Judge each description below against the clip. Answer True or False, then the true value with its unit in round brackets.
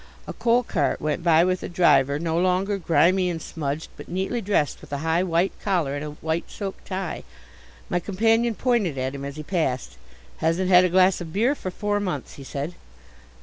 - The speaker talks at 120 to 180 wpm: False (200 wpm)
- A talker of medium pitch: True (175 Hz)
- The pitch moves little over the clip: False (4.0 semitones)